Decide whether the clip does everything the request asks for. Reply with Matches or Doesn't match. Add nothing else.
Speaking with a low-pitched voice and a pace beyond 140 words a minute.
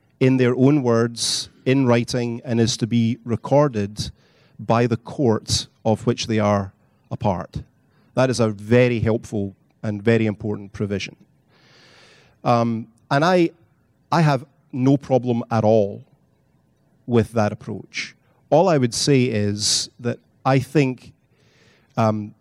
Doesn't match